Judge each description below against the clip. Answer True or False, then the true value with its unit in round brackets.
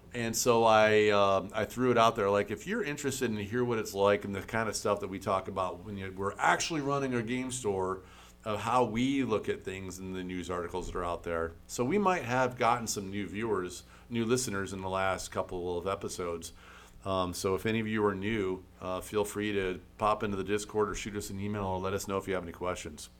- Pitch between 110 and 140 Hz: False (100 Hz)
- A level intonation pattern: False (3.3 semitones)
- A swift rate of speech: True (250 wpm)